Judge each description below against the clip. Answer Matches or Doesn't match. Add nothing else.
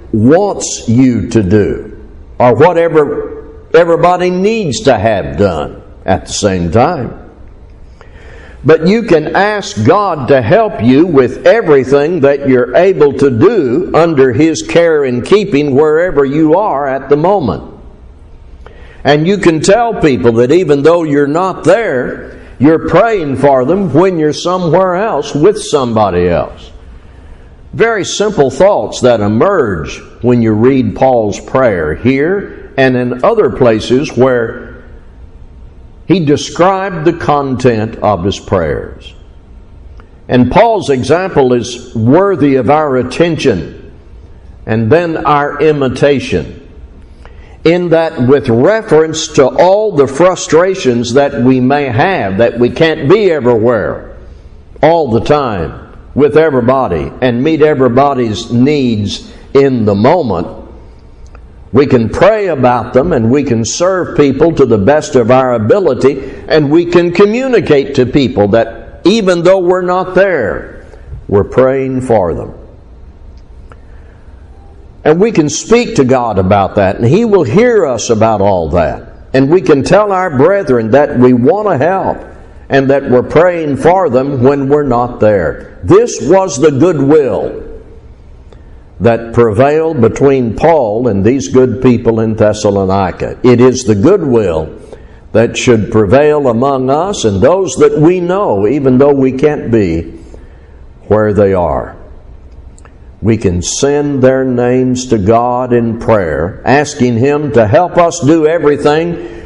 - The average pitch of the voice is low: Matches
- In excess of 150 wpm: Doesn't match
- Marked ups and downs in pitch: Matches